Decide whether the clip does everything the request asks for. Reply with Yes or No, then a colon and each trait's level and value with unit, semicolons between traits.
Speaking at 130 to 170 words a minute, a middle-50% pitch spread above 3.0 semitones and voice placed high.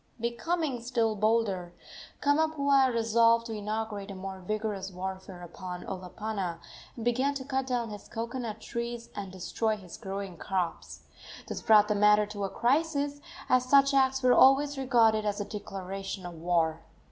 Yes: average, 155 wpm; average, 4.6 semitones; high, 220 Hz